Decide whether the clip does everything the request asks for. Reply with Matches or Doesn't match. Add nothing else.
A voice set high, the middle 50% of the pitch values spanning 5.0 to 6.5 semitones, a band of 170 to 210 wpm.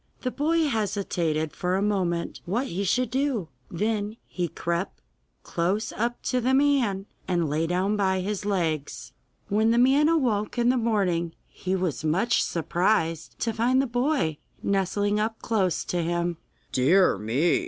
Doesn't match